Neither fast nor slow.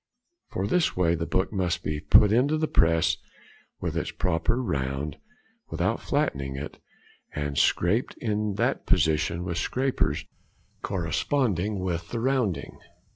No: slow, 130 wpm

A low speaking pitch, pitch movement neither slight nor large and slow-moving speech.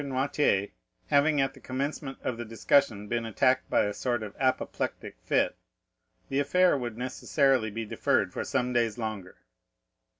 No: low, 125 Hz; average, 3.7 semitones; average, 155 wpm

